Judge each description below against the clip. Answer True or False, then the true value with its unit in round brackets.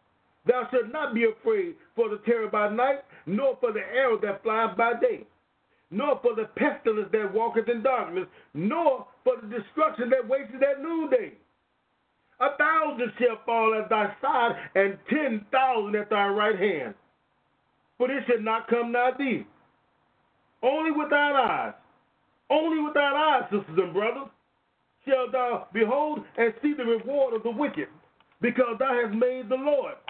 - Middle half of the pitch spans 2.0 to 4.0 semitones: False (4.4 semitones)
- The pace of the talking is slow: False (165 wpm)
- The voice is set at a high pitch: True (250 Hz)